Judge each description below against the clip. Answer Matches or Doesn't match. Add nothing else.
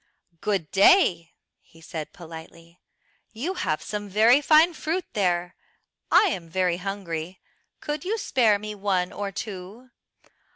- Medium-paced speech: Doesn't match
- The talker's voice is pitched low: Doesn't match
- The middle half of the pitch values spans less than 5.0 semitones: Doesn't match